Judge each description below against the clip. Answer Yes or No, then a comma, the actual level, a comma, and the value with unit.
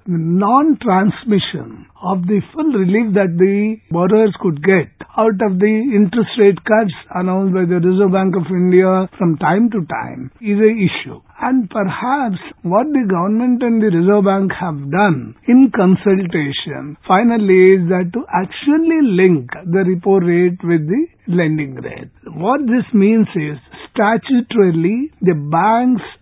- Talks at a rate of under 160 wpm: Yes, average, 145 wpm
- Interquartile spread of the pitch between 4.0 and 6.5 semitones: No, average, 3.6 semitones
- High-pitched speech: Yes, high, 195 Hz